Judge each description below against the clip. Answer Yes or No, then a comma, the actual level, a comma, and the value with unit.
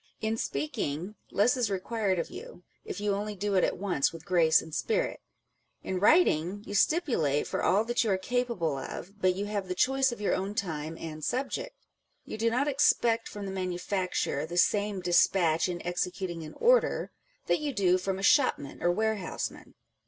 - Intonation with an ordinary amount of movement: Yes, average, 4.2 semitones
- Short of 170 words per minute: No, average, 190 wpm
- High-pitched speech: Yes, high, 195 Hz